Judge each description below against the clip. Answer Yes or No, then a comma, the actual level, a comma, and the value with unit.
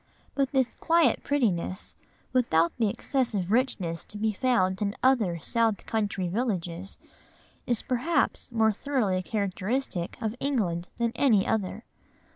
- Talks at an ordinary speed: No, slow, 125 wpm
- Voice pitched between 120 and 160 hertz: No, high, 220 Hz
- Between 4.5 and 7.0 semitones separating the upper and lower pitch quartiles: Yes, average, 5.2 semitones